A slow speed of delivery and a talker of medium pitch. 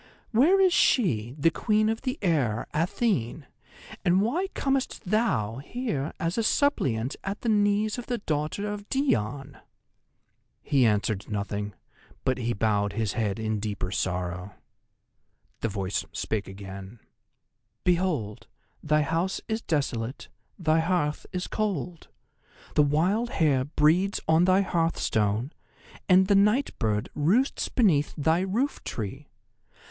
Yes: slow, 130 wpm; medium, 155 Hz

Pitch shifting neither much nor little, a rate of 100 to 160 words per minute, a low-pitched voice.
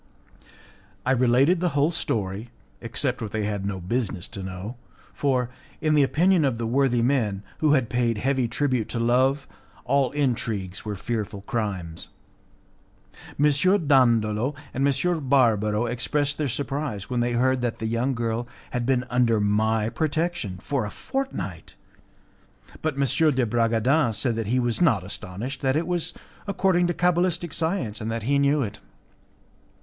Yes: average, 4.3 semitones; average, 155 wpm; low, 125 Hz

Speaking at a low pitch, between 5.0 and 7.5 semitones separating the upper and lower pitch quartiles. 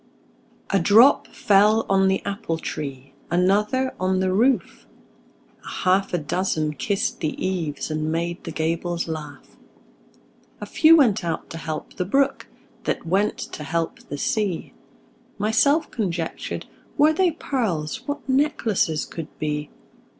No: medium, 185 Hz; average, 5.3 semitones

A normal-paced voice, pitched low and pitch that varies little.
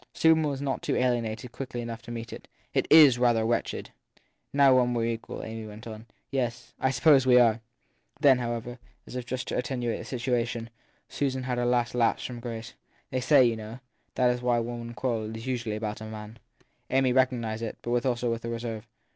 No: fast, 220 wpm; low, 120 Hz; narrow, 1.8 semitones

